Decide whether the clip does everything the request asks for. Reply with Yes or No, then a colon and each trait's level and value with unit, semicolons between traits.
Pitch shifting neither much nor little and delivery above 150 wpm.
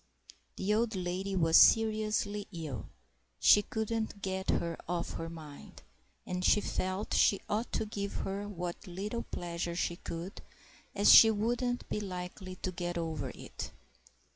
No: average, 3.4 semitones; average, 145 wpm